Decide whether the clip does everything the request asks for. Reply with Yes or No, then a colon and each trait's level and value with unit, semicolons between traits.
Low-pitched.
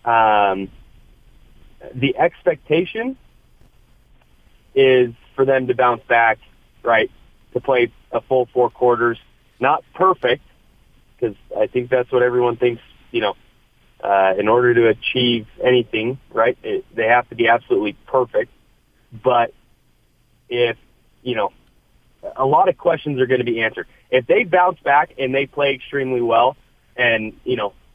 Yes: low, 125 Hz